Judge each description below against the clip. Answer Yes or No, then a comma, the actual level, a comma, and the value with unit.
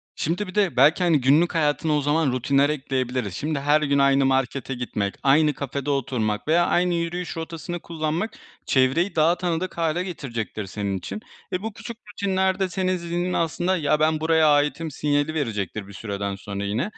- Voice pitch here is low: No, medium, 150 Hz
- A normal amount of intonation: Yes, average, 4.6 semitones